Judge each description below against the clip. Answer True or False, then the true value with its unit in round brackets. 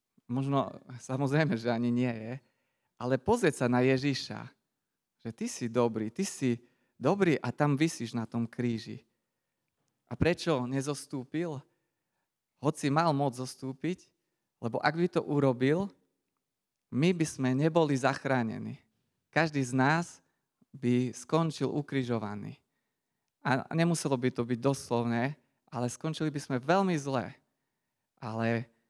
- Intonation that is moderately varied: True (4.0 semitones)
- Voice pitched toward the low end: True (130 Hz)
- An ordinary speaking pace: True (125 wpm)